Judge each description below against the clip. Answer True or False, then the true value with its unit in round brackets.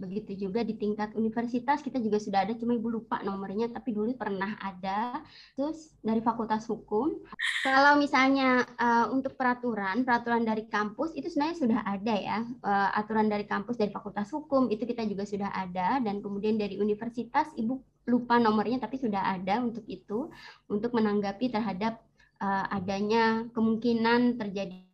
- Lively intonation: False (2.9 semitones)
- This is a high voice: True (225 Hz)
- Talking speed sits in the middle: False (155 wpm)